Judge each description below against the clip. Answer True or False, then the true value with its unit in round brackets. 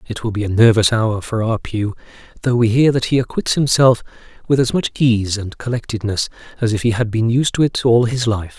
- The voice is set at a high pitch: False (115 Hz)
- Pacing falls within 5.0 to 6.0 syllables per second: True (5.5 syllables/s)